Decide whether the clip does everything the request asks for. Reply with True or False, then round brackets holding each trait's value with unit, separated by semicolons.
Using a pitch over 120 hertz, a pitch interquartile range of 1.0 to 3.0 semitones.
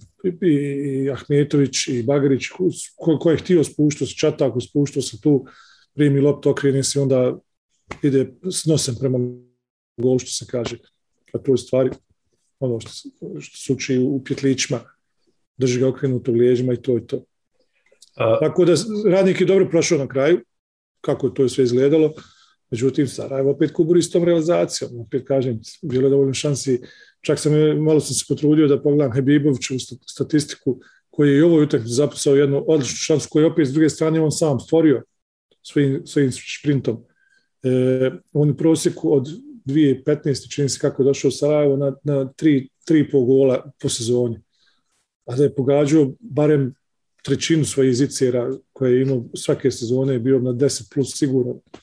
True (140 Hz; 2.7 semitones)